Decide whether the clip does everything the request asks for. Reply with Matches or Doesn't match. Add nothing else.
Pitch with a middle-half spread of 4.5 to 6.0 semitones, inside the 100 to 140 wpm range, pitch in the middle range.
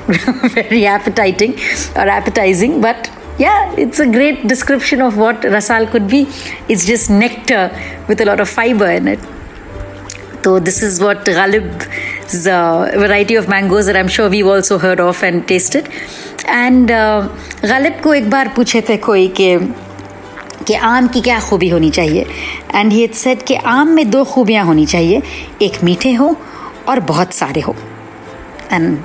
Doesn't match